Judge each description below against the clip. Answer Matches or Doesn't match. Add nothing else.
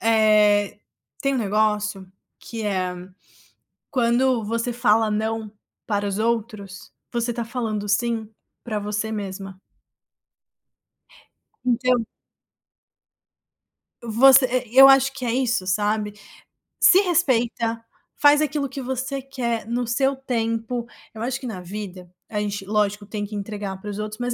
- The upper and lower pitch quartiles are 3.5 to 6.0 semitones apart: Doesn't match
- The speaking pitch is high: Matches